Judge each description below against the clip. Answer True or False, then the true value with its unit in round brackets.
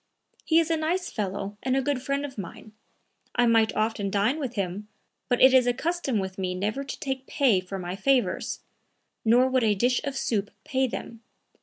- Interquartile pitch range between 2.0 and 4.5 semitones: False (4.9 semitones)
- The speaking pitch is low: False (245 Hz)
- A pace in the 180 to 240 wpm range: True (200 wpm)